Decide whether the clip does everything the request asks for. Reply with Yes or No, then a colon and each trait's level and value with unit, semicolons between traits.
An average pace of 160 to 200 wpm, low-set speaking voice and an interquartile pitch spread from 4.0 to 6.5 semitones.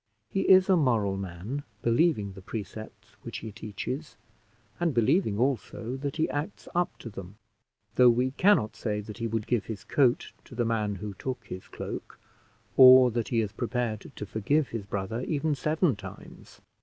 Yes: average, 175 wpm; low, 115 Hz; average, 5.1 semitones